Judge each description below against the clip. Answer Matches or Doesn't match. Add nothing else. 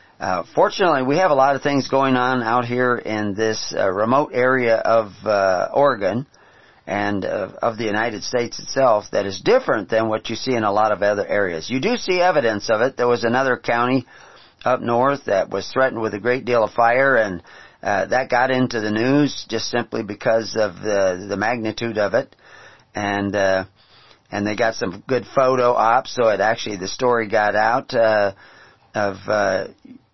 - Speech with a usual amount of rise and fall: Matches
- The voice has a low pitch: Matches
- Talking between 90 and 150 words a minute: Doesn't match